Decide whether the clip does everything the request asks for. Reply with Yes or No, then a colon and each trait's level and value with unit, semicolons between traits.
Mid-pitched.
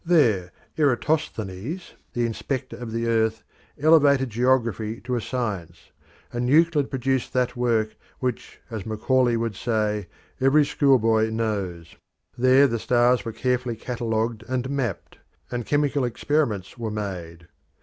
No: low, 120 Hz